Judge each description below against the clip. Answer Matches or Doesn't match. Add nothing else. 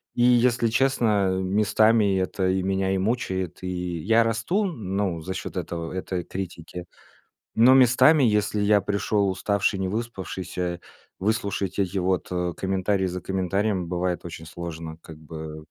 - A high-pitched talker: Doesn't match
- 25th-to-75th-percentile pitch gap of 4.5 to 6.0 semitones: Doesn't match